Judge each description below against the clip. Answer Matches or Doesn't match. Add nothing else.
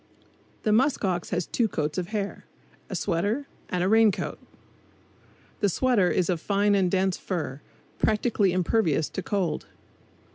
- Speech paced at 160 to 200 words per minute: Doesn't match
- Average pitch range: Matches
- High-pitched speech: Matches